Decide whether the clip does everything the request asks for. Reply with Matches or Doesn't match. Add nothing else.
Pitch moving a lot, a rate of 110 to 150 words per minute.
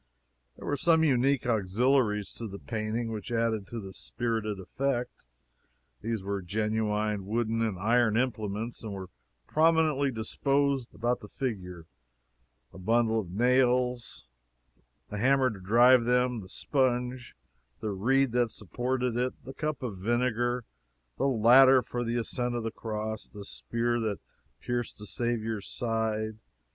Doesn't match